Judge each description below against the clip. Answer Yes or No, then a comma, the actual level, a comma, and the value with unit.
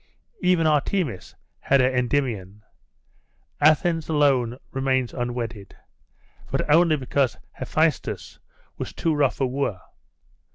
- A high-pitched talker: No, low, 135 Hz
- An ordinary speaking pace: No, slow, 100 wpm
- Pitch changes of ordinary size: Yes, average, 3.8 semitones